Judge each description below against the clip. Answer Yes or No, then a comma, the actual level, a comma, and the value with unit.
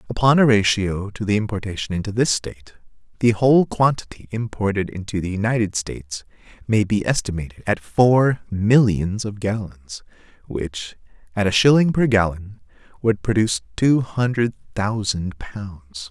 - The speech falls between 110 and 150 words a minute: Yes, average, 140 wpm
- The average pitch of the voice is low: Yes, low, 105 Hz